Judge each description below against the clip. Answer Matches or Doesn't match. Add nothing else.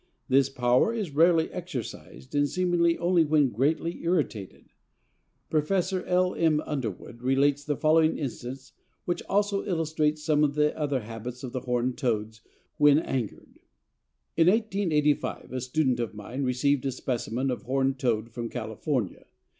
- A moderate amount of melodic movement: Matches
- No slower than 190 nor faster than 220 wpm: Doesn't match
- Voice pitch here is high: Doesn't match